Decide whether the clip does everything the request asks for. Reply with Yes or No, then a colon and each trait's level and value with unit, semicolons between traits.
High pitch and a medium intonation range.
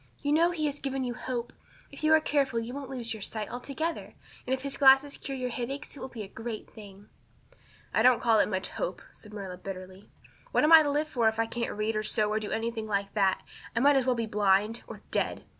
Yes: high, 235 Hz; average, 4.4 semitones